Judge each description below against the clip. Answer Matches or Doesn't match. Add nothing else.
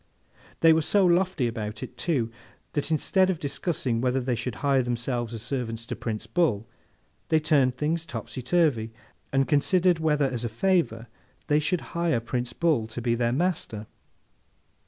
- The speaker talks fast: Doesn't match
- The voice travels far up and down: Matches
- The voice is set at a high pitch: Doesn't match